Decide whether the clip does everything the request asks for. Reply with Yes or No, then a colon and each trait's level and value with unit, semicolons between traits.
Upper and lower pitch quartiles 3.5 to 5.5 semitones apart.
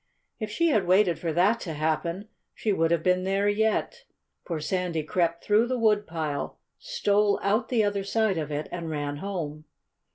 Yes: average, 4.4 semitones